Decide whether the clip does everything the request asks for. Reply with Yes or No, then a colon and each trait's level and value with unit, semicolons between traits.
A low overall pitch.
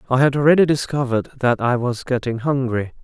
Yes: low, 130 Hz